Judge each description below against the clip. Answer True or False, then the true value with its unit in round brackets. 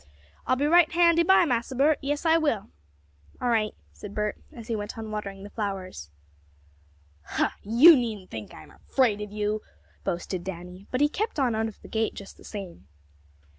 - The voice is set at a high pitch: True (220 Hz)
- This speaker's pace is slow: False (185 wpm)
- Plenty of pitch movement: True (5.9 semitones)